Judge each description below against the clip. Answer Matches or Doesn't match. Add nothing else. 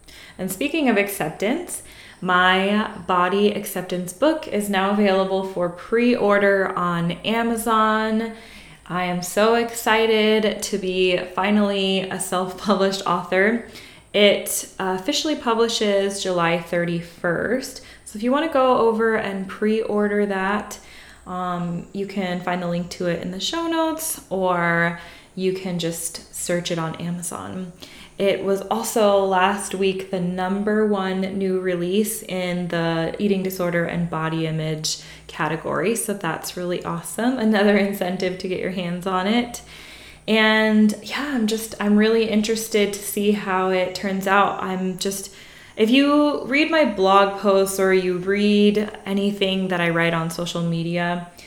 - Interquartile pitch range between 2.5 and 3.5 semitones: Matches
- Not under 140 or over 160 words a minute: Matches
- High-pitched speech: Matches